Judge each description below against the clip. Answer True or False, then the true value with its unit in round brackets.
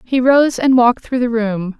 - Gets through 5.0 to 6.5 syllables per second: False (4.7 syllables/s)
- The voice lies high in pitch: True (240 Hz)